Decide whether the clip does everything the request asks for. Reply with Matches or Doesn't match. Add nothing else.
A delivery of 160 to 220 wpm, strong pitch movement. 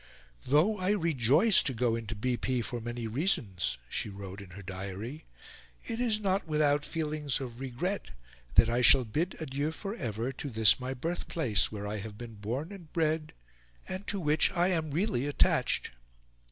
Matches